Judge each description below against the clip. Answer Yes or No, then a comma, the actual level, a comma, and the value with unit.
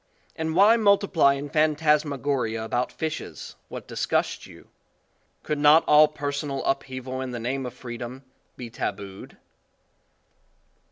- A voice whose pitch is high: No, medium, 140 Hz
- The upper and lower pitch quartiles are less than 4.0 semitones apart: Yes, average, 3.5 semitones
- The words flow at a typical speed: No, slow, 120 wpm